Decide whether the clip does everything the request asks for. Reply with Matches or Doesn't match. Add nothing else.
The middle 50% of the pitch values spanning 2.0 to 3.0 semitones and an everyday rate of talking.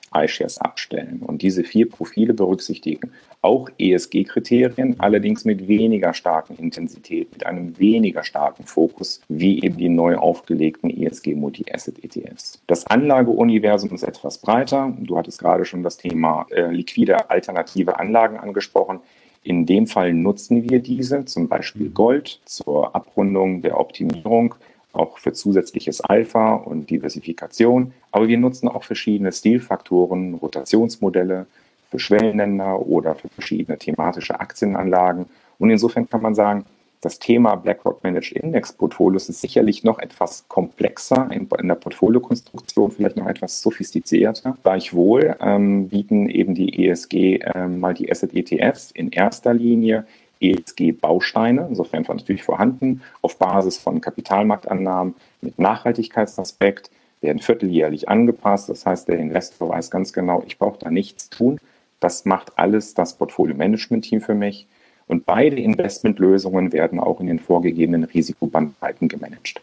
Doesn't match